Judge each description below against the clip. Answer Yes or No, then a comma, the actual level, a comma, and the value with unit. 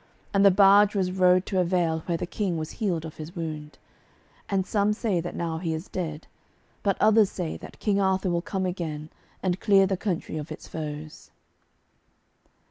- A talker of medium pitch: Yes, medium, 180 Hz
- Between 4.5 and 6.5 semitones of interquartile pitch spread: No, average, 3.3 semitones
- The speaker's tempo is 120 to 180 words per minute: No, average, 190 wpm